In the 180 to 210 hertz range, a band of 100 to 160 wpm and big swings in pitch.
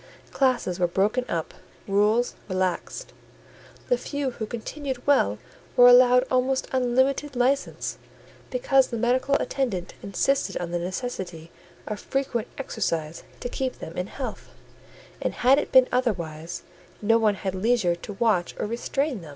No: high, 235 Hz; average, 145 wpm; wide, 5.8 semitones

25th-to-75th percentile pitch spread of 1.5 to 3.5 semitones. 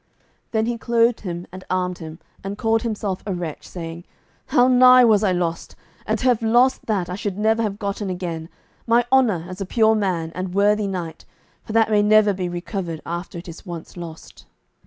No: average, 4.0 semitones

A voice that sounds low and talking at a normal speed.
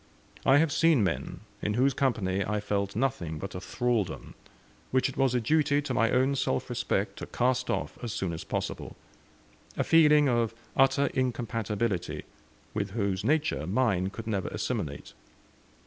Yes: low, 115 Hz; average, 160 wpm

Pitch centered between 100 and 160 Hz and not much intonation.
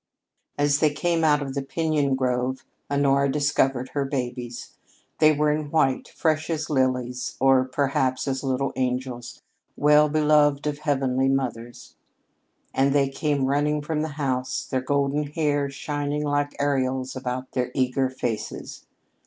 Yes: medium, 140 Hz; narrow, 2.2 semitones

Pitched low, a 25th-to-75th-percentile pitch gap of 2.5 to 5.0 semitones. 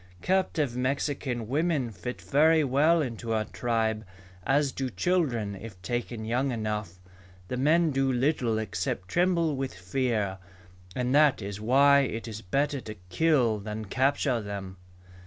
Yes: low, 125 Hz; average, 4.7 semitones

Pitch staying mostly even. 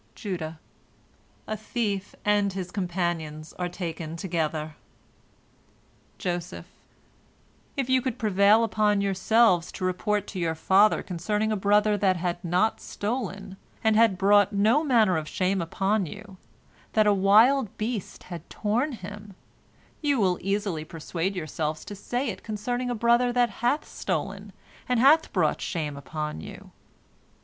No: average, 3.7 semitones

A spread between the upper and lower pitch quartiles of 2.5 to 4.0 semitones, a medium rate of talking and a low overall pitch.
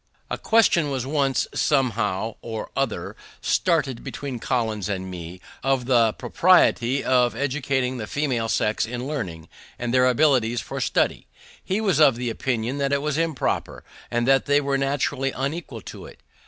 Yes: average, 3.5 semitones; average, 155 wpm; low, 130 Hz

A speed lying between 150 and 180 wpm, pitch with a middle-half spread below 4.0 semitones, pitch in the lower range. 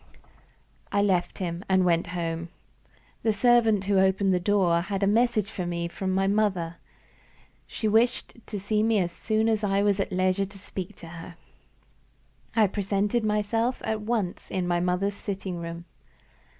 No: average, 165 wpm; average, 2.9 semitones; high, 195 Hz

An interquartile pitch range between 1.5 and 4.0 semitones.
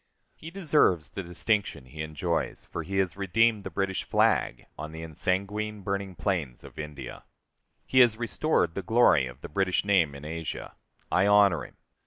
No: average, 4.5 semitones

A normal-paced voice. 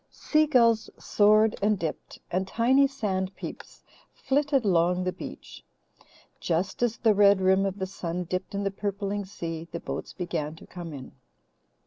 Yes: average, 160 wpm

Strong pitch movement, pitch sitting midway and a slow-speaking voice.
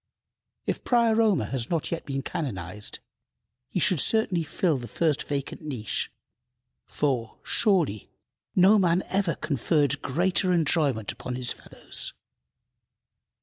Yes: wide, 5.9 semitones; medium, 155 Hz; slow, 120 wpm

